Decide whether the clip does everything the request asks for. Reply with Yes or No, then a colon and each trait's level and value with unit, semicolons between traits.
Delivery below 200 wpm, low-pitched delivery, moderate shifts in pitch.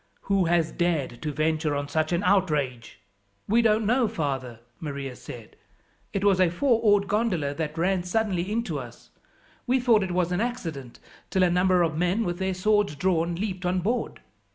No: average, 180 wpm; medium, 180 Hz; average, 4.6 semitones